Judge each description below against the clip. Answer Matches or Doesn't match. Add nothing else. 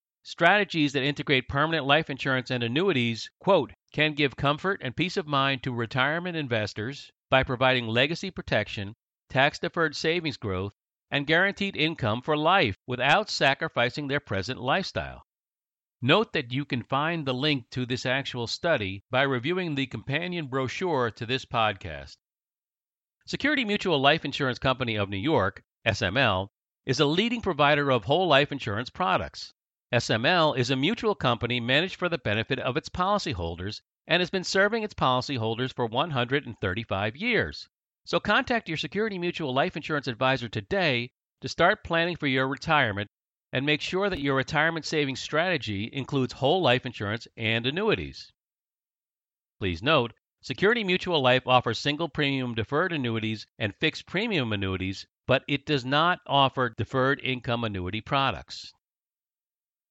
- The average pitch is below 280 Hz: Matches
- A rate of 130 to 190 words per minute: Matches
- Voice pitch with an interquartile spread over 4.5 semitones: Matches